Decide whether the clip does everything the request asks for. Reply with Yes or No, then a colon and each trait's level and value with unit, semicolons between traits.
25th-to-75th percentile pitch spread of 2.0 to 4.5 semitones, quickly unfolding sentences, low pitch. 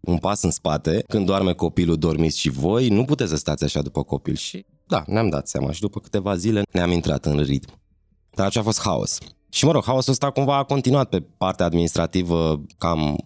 No: average, 5.3 semitones; fast, 215 wpm; very low, 85 Hz